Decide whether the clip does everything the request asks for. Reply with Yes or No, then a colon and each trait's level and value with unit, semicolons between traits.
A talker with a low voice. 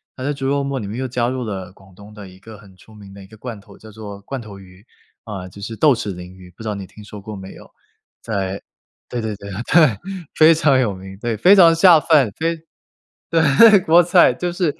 Yes: low, 110 Hz